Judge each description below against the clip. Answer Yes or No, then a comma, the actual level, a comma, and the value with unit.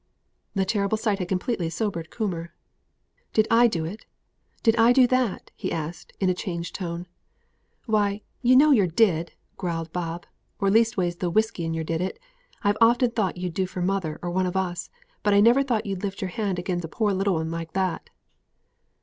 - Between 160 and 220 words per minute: Yes, average, 195 wpm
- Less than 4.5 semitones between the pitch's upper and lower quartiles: Yes, average, 4.1 semitones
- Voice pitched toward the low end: No, high, 190 Hz